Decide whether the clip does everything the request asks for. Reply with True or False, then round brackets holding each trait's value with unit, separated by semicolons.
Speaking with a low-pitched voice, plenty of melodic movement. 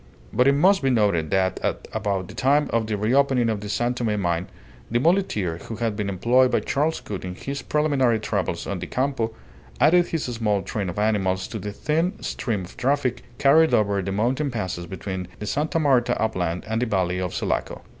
True (110 Hz; 5.8 semitones)